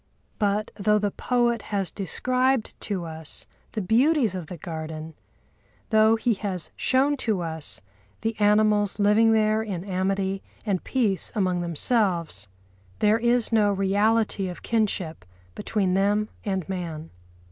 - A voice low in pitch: No, high, 205 Hz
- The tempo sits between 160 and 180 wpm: No, slow, 135 wpm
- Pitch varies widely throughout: No, average, 3.3 semitones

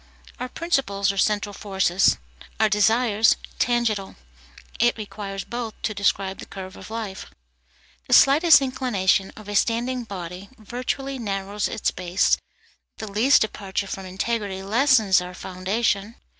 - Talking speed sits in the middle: No, slow, 130 wpm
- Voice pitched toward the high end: Yes, high, 210 Hz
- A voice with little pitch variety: No, average, 3.5 semitones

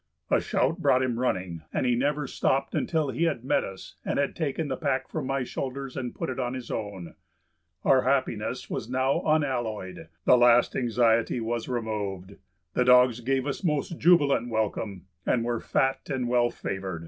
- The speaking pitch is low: Yes, low, 125 Hz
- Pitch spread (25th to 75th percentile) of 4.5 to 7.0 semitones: No, average, 3.2 semitones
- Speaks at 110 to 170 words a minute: No, average, 180 wpm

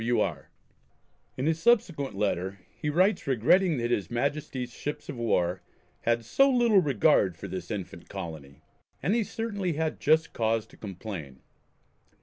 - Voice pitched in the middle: No, low, 120 Hz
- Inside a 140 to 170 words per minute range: Yes, average, 150 wpm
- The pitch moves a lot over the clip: Yes, wide, 8.7 semitones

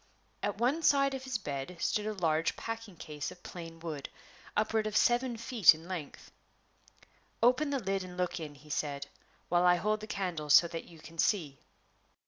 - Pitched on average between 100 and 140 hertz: No, medium, 180 Hz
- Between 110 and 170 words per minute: No, average, 185 wpm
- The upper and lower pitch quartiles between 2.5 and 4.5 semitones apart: No, wide, 5.6 semitones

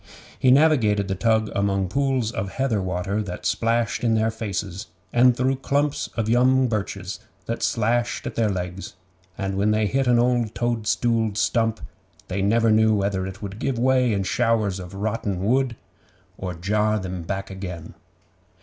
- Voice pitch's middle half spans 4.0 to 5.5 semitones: No, average, 3.5 semitones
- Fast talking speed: No, average, 165 wpm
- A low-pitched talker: Yes, low, 110 Hz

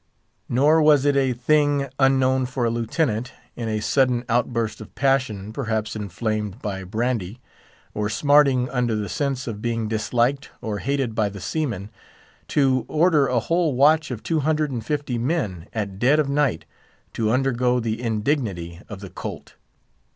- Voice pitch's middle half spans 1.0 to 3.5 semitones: No, average, 4.2 semitones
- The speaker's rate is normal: Yes, average, 160 wpm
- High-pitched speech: No, low, 125 Hz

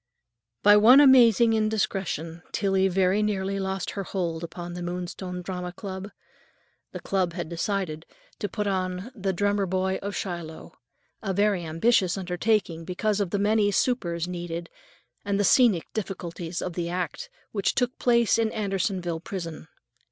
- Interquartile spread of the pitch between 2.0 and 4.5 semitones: Yes, average, 2.9 semitones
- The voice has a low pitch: No, high, 190 Hz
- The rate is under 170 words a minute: Yes, average, 150 wpm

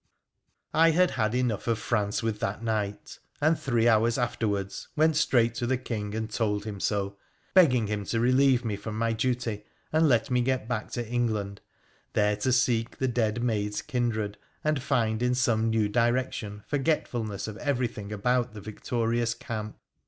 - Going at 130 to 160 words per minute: No, average, 170 wpm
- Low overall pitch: Yes, low, 115 Hz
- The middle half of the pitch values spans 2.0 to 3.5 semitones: Yes, average, 2.8 semitones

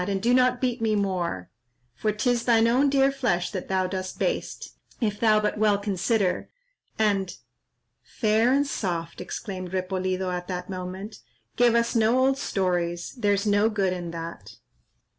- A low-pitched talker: No, high, 205 Hz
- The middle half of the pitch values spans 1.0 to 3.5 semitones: No, average, 4.0 semitones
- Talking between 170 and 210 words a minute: No, average, 160 wpm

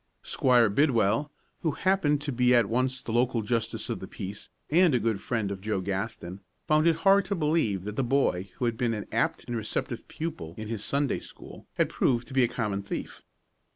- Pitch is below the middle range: Yes, low, 120 Hz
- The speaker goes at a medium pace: No, fast, 210 wpm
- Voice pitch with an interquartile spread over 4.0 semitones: Yes, average, 5.3 semitones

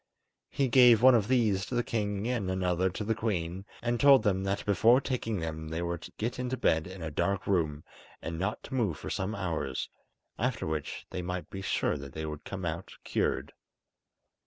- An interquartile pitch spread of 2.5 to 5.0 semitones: No, wide, 5.4 semitones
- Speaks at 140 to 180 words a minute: No, fast, 205 wpm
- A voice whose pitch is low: Yes, very low, 95 Hz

